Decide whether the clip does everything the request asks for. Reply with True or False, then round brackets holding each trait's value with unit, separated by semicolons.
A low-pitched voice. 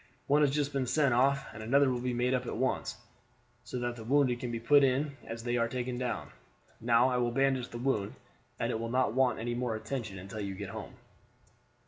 True (125 Hz)